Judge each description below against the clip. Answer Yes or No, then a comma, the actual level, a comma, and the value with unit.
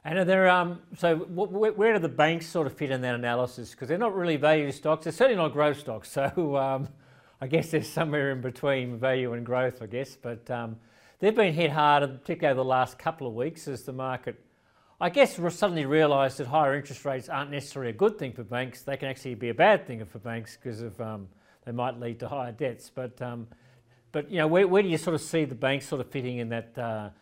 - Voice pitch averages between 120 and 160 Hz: Yes, low, 135 Hz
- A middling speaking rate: No, fast, 240 wpm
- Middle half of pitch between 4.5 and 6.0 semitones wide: Yes, average, 4.8 semitones